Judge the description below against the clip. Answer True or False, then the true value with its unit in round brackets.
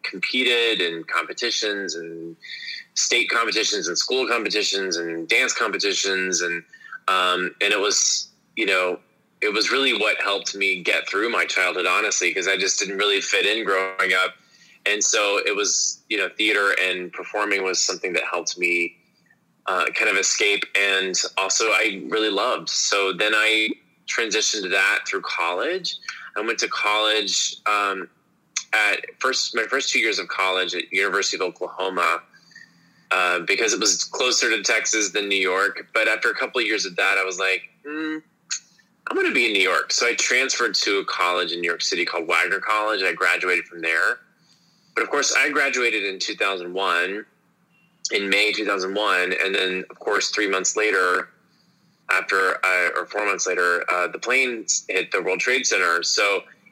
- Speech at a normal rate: True (175 wpm)